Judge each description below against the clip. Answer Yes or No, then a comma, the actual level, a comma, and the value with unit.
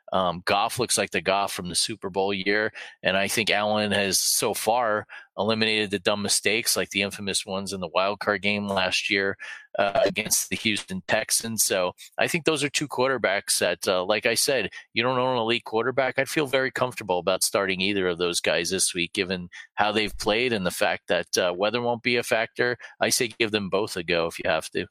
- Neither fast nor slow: No, fast, 225 wpm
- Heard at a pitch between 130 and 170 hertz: No, low, 105 Hz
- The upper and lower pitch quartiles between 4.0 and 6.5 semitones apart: No, average, 3.2 semitones